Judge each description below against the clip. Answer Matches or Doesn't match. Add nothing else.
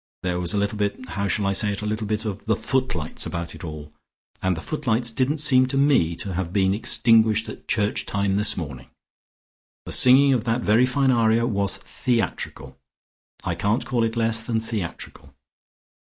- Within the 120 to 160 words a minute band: Doesn't match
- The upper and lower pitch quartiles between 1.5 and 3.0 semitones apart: Doesn't match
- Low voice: Matches